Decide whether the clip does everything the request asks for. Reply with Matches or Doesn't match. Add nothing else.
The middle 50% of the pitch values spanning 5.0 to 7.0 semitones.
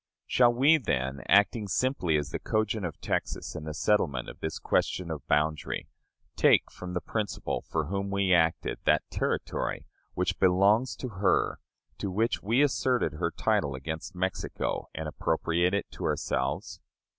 Matches